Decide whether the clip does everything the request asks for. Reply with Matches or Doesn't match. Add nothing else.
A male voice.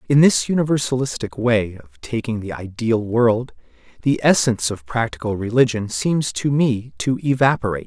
Matches